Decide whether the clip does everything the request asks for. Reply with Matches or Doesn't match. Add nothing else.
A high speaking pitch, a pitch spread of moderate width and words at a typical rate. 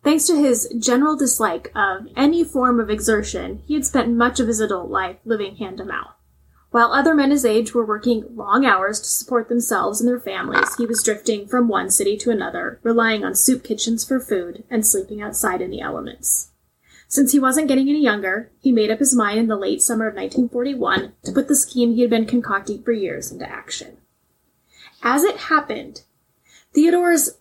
Matches